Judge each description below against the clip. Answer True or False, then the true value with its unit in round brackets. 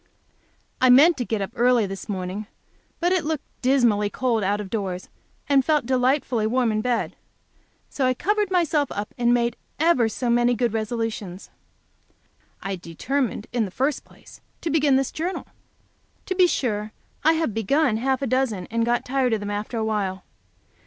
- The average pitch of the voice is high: True (240 Hz)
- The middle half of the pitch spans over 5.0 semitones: False (4.4 semitones)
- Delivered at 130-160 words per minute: False (175 wpm)